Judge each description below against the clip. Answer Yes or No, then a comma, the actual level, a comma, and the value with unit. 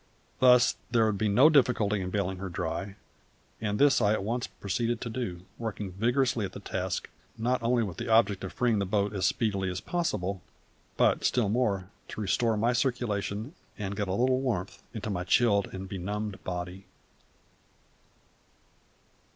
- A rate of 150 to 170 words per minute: Yes, average, 165 wpm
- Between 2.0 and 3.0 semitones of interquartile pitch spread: No, average, 3.6 semitones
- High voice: No, low, 105 Hz